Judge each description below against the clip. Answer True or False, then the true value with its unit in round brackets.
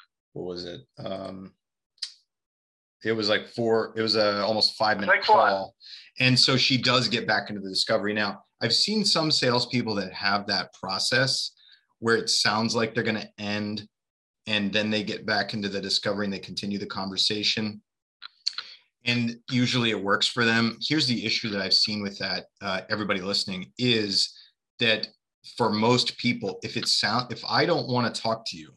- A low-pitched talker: True (110 Hz)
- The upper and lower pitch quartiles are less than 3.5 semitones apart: True (3.0 semitones)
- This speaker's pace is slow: False (180 wpm)